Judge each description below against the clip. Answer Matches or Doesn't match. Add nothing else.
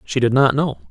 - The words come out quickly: Matches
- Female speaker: Doesn't match